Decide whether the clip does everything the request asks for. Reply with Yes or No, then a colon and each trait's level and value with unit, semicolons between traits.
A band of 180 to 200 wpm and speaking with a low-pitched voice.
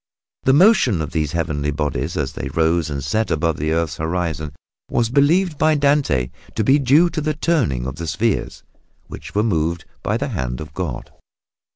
Yes: average, 185 wpm; very low, 85 Hz